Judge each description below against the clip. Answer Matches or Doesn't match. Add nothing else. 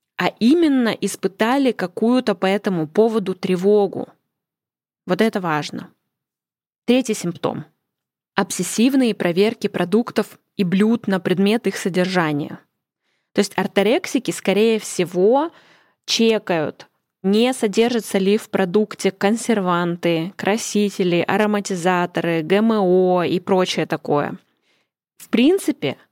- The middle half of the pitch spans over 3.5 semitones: Doesn't match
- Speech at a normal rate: Doesn't match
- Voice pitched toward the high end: Matches